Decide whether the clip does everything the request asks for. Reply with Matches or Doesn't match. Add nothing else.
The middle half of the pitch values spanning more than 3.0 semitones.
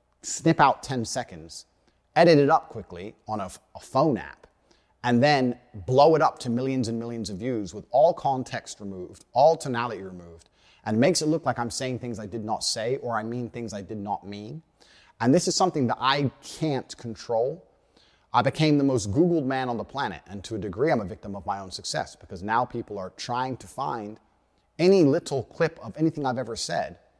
Matches